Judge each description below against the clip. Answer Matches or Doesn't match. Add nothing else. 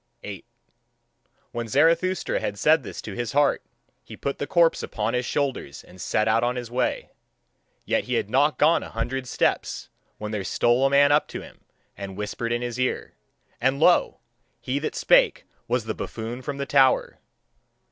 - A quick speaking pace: Doesn't match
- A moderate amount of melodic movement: Matches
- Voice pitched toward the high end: Doesn't match